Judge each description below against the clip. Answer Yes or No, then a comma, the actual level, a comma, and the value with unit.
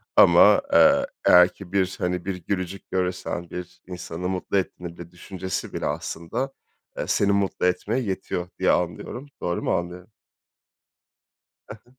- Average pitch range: No, narrow, 2.0 semitones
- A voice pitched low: Yes, very low, 90 Hz